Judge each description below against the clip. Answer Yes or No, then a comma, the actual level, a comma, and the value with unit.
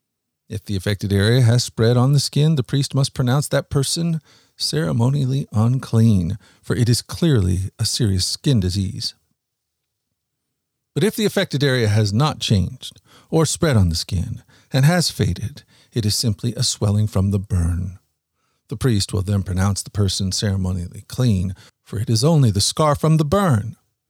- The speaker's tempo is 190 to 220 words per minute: No, average, 165 wpm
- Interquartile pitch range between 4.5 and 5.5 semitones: Yes, average, 5.2 semitones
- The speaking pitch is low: Yes, low, 115 Hz